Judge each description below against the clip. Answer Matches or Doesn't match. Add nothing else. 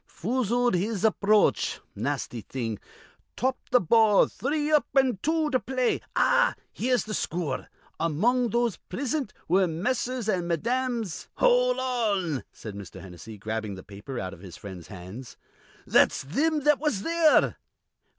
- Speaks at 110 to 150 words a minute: Matches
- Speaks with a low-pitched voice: Doesn't match